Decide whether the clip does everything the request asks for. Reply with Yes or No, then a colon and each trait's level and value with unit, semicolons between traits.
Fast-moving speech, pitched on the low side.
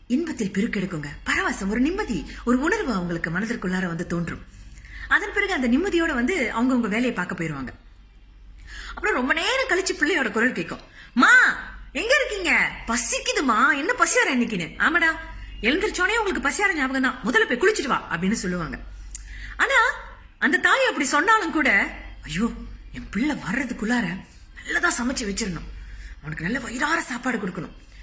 No: fast, 140 wpm; high, 245 Hz